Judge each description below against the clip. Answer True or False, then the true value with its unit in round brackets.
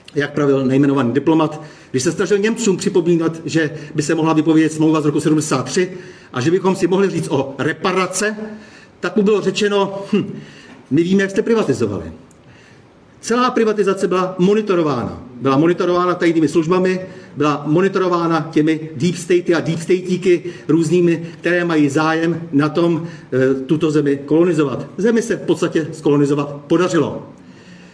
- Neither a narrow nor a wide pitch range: True (3.3 semitones)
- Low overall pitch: False (165 Hz)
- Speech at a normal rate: True (145 wpm)